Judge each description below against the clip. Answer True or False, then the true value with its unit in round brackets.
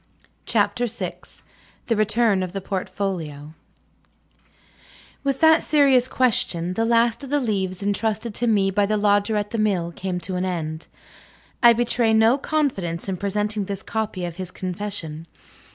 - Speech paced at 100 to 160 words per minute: True (150 wpm)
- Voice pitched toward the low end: False (205 Hz)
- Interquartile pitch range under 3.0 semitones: False (3.8 semitones)